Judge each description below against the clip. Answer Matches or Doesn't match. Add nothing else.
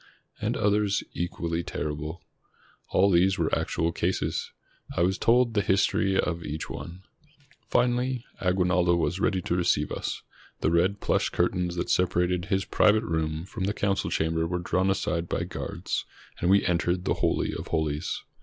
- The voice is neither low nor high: Doesn't match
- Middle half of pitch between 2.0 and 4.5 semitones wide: Matches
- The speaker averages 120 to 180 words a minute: Matches